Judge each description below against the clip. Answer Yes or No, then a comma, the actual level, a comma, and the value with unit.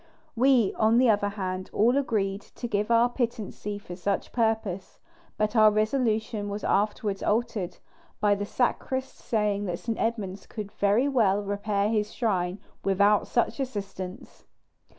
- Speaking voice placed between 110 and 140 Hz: No, high, 210 Hz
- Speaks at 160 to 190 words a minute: No, average, 145 wpm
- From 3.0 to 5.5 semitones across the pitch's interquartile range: No, narrow, 2.4 semitones